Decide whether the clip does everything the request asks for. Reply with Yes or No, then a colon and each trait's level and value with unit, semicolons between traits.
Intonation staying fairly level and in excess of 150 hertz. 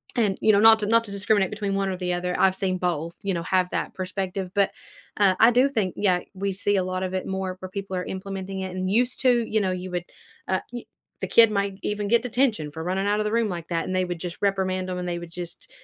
Yes: narrow, 2.2 semitones; high, 190 Hz